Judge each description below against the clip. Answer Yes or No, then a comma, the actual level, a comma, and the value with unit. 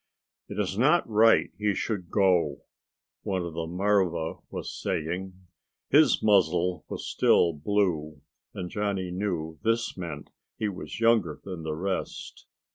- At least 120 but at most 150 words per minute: Yes, slow, 135 wpm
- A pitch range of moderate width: Yes, average, 3.6 semitones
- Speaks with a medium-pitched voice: No, very low, 95 Hz